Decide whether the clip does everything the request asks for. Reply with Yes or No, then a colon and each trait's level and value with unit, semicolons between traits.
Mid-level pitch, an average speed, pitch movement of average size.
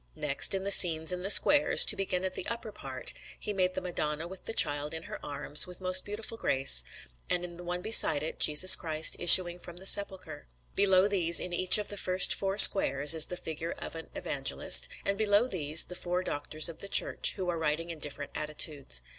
No: medium, 175 Hz; fast, 215 wpm; average, 3.8 semitones